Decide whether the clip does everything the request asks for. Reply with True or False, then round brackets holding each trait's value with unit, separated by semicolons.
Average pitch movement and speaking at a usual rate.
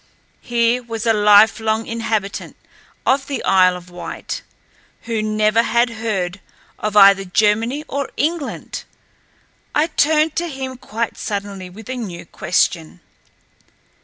False (3.7 semitones; 125 wpm)